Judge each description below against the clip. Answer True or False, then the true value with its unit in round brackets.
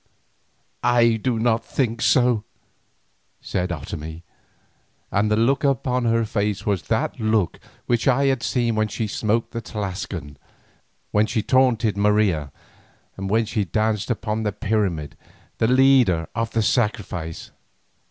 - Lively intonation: False (2.6 semitones)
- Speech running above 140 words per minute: False (135 wpm)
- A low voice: True (110 Hz)